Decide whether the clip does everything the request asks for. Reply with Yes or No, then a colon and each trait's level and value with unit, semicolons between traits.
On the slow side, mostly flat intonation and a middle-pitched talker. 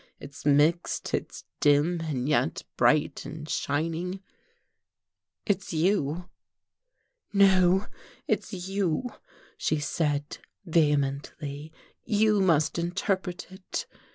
No: slow, 90 wpm; average, 4.3 semitones; medium, 165 Hz